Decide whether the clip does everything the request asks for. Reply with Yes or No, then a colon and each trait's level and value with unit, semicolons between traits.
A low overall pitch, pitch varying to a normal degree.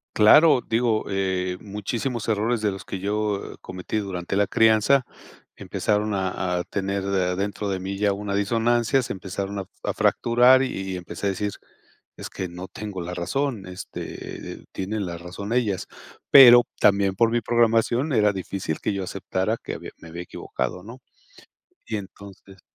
Yes: low, 100 Hz; average, 3.1 semitones